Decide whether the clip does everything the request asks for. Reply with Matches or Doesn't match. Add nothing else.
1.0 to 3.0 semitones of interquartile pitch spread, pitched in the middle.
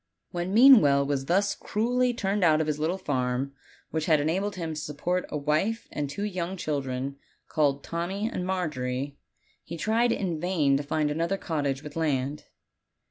Doesn't match